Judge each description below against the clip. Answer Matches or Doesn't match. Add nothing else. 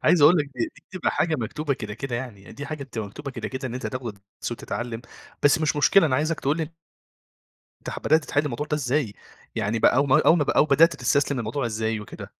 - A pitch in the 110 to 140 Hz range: Matches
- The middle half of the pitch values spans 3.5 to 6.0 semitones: Matches